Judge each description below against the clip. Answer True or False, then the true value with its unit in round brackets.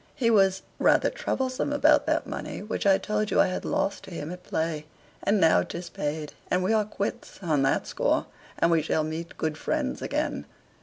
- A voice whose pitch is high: False (180 Hz)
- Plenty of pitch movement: False (4.7 semitones)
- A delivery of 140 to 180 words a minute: False (200 wpm)